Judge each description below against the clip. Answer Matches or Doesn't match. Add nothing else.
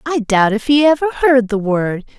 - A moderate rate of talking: Doesn't match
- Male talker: Doesn't match